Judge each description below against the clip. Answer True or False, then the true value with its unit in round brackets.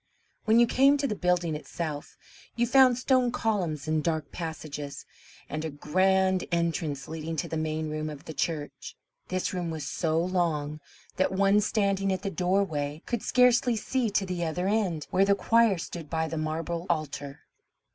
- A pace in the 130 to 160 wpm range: False (175 wpm)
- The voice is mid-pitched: True (170 Hz)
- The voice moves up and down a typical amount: True (4.2 semitones)